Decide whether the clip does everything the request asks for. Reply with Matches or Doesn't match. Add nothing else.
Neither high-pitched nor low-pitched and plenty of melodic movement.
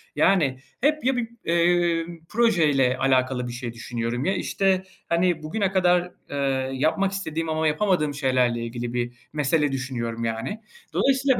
Matches